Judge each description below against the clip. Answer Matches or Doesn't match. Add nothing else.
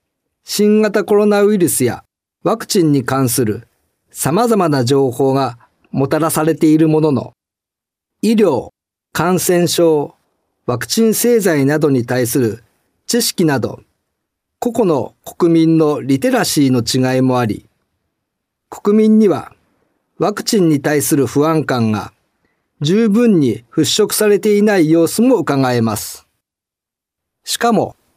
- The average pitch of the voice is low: Doesn't match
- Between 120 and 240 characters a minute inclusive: Matches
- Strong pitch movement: Matches